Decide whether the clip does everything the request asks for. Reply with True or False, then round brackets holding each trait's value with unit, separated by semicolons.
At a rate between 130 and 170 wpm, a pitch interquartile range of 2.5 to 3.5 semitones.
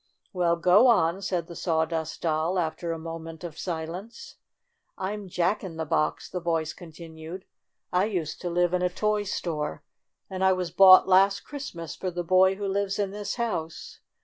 False (180 wpm; 2.8 semitones)